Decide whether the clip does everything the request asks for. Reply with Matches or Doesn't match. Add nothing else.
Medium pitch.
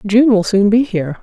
Doesn't match